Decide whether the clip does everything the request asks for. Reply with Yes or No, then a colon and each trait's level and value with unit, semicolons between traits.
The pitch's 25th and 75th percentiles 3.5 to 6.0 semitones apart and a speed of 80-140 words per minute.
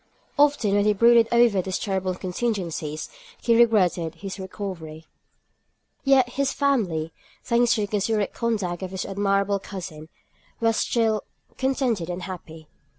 Yes: average, 4.4 semitones; slow, 135 wpm